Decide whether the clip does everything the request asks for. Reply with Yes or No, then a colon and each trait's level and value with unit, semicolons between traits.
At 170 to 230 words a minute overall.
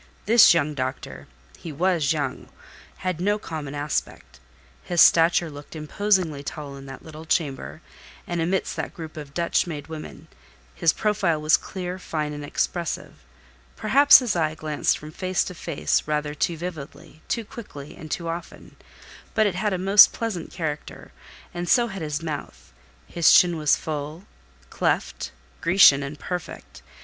No: average, 155 wpm